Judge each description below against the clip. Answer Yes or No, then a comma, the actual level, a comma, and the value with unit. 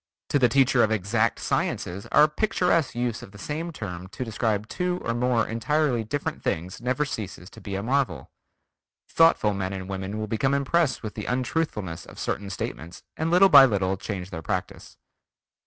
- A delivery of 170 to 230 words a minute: Yes, average, 180 wpm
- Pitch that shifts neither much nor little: No, wide, 6.1 semitones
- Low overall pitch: Yes, low, 115 Hz